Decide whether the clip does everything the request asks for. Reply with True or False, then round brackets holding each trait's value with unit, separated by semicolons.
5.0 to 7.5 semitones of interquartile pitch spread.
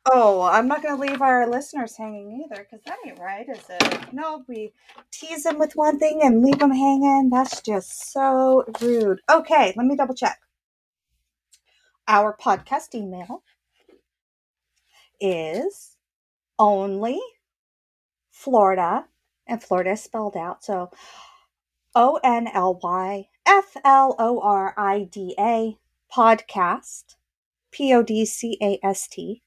True (5.3 semitones)